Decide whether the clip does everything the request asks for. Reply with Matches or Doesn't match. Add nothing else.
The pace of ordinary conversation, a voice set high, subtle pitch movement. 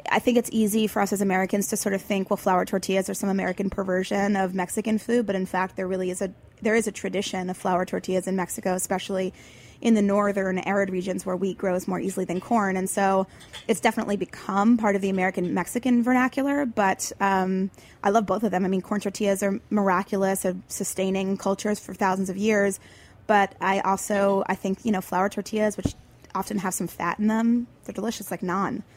Doesn't match